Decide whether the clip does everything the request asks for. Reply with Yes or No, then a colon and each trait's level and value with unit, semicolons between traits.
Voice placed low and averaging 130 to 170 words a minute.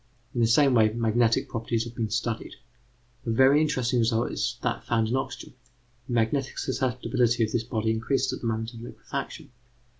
No: low, 115 Hz; average, 180 wpm